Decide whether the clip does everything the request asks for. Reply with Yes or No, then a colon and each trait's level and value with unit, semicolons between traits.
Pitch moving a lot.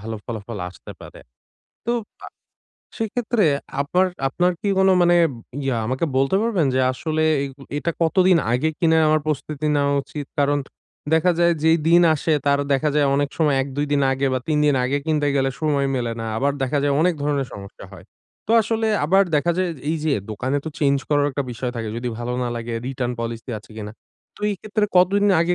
No: average, 4.3 semitones